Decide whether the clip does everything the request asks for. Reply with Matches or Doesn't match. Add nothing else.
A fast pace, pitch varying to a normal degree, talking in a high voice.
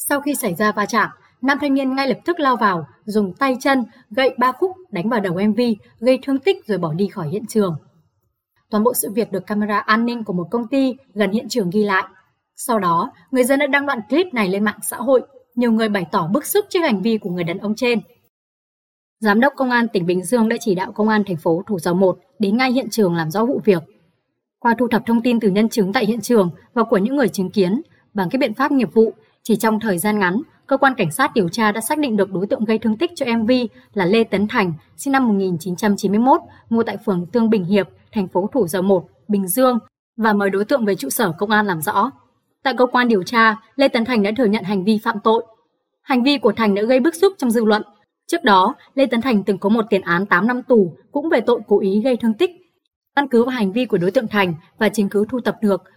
Matches